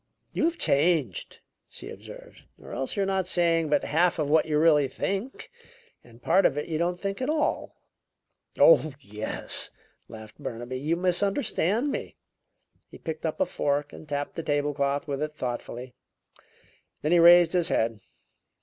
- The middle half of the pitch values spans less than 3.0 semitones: No, average, 4.1 semitones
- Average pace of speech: Yes, average, 165 wpm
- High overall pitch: No, medium, 155 Hz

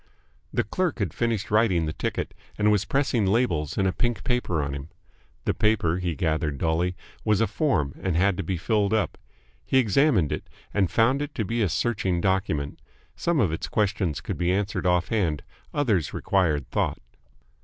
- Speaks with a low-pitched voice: Yes, very low, 95 Hz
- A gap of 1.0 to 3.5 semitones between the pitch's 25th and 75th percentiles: No, average, 5.2 semitones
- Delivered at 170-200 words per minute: Yes, average, 185 wpm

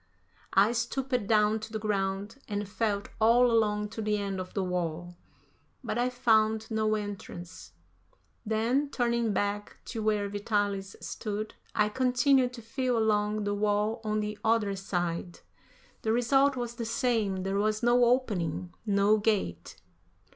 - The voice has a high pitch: Yes, high, 215 Hz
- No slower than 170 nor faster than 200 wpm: No, average, 145 wpm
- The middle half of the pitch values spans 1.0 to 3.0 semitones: Yes, narrow, 2.4 semitones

